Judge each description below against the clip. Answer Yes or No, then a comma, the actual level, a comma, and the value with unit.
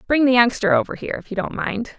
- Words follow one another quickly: Yes, fast, 270 wpm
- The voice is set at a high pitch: Yes, high, 235 Hz